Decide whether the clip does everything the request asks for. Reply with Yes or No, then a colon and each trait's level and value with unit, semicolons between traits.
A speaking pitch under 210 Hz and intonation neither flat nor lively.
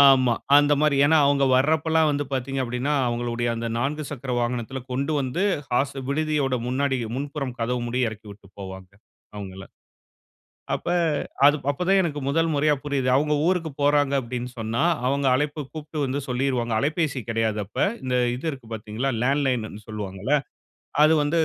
Yes: low, 135 Hz; average, 3.5 semitones